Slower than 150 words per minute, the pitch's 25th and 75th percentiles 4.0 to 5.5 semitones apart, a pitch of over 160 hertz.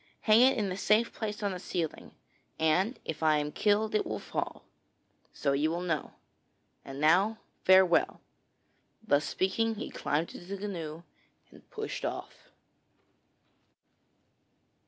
Yes: average, 140 wpm; average, 5.1 semitones; medium, 185 Hz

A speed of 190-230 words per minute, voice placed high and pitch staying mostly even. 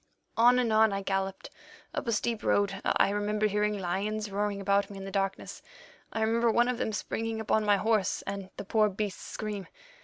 Yes: average, 195 wpm; high, 210 Hz; narrow, 1.9 semitones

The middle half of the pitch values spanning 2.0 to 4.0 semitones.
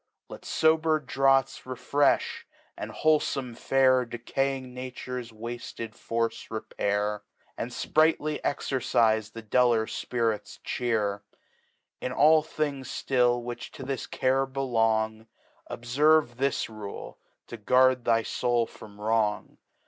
Yes: average, 3.1 semitones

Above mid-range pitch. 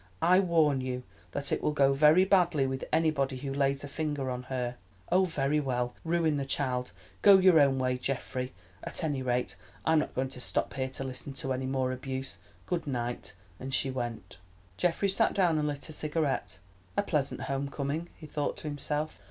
No: medium, 140 Hz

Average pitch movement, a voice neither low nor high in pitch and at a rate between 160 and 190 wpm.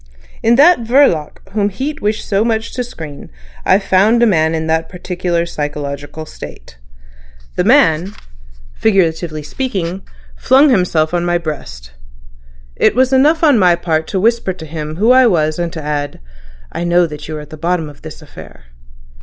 No: wide, 6.0 semitones; medium, 175 Hz; average, 170 wpm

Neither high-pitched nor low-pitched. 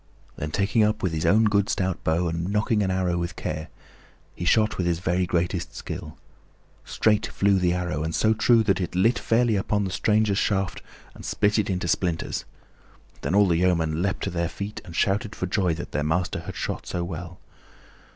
No: very low, 90 Hz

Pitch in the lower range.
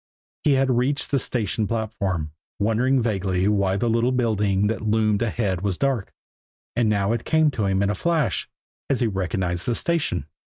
Yes: low, 110 Hz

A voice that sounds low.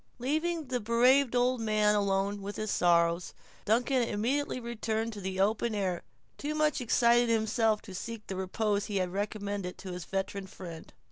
No: high, 215 Hz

